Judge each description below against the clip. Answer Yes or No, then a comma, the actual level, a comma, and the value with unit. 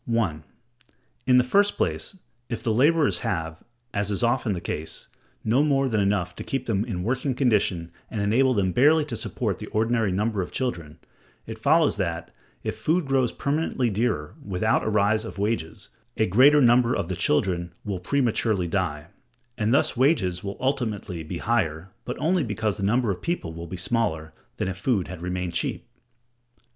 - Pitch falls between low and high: No, low, 110 Hz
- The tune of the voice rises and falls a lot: Yes, wide, 5.7 semitones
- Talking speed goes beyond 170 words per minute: Yes, average, 180 wpm